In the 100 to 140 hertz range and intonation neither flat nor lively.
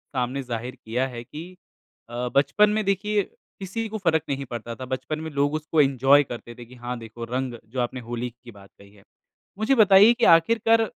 No: low, 135 Hz; wide, 8.0 semitones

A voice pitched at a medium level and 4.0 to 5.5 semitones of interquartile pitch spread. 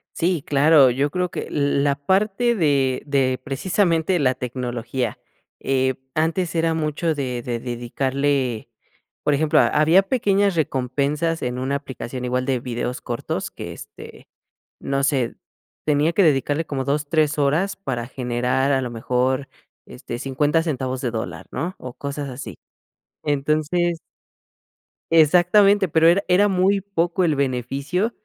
Yes: medium, 145 Hz; average, 4.4 semitones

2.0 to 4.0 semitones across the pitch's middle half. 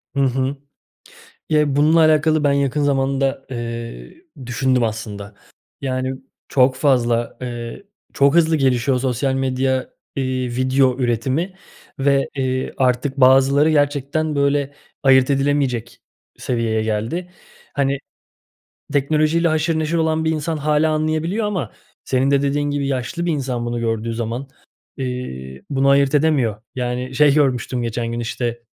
Yes: average, 2.9 semitones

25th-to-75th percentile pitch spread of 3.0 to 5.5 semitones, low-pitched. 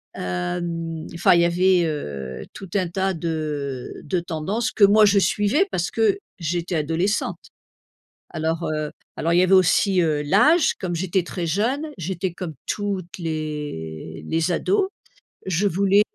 No: average, 3.7 semitones; medium, 175 Hz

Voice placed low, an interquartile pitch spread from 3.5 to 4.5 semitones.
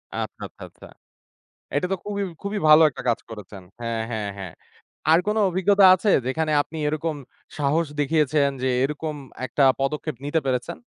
No: medium, 150 Hz; average, 4.1 semitones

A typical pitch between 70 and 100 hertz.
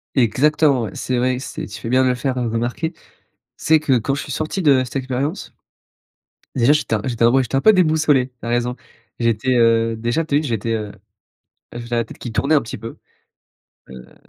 No: low, 125 Hz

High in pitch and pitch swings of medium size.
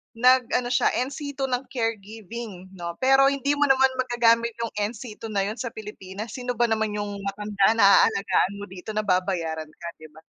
Yes: high, 220 Hz; average, 3.9 semitones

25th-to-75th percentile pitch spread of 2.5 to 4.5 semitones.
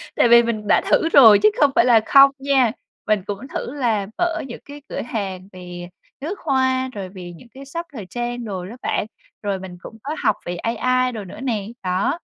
No: average, 5.3 semitones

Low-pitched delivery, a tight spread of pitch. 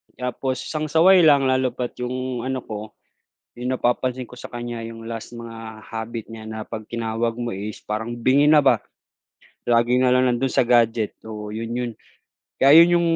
Yes: low, 120 Hz; narrow, 2.3 semitones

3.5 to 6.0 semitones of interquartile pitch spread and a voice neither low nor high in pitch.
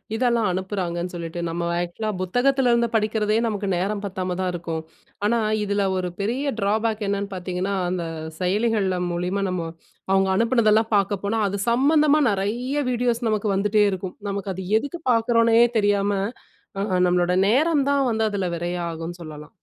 No: average, 4.0 semitones; high, 200 Hz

